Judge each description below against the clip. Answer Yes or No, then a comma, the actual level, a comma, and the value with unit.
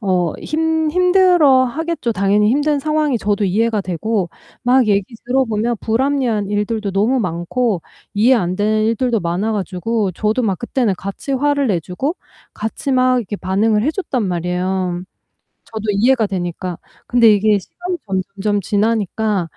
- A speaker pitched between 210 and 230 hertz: Yes, high, 220 Hz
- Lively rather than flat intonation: No, average, 4.8 semitones